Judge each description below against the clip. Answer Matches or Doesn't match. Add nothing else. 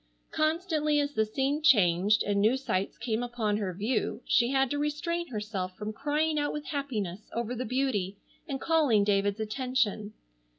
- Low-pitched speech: Doesn't match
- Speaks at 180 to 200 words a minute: Doesn't match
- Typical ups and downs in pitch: Doesn't match